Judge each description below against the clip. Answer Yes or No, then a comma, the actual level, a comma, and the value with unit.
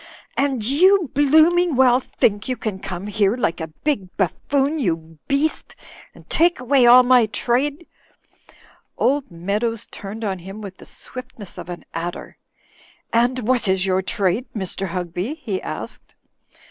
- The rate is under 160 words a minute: Yes, average, 150 wpm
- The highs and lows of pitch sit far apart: Yes, wide, 6.0 semitones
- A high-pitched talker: Yes, high, 230 Hz